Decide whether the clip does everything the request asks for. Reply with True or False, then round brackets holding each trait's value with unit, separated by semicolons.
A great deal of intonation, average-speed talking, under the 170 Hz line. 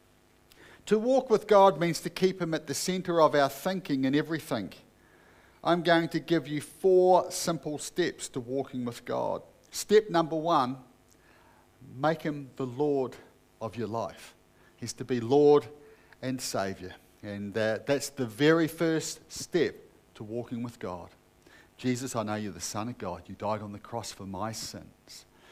True (6.6 semitones; 165 wpm; 135 Hz)